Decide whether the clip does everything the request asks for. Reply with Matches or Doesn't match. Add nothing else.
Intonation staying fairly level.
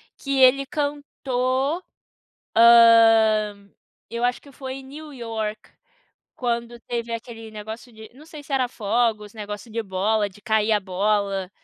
Doesn't match